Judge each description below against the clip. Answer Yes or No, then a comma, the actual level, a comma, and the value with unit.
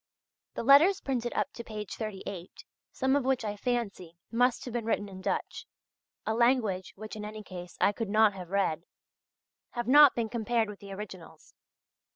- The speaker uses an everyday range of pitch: Yes, average, 3.6 semitones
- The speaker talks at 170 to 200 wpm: Yes, average, 180 wpm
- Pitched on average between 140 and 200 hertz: No, high, 215 Hz